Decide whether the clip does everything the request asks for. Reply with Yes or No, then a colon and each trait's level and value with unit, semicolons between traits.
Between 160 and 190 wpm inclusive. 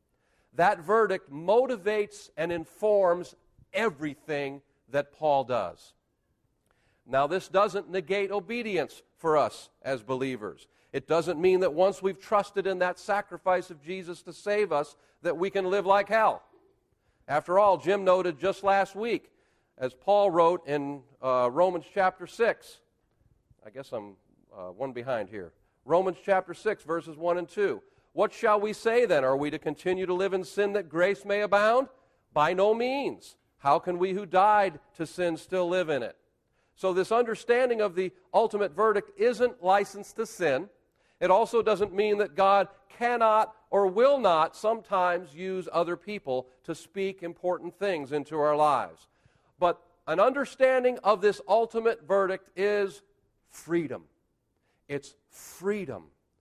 No: average, 150 wpm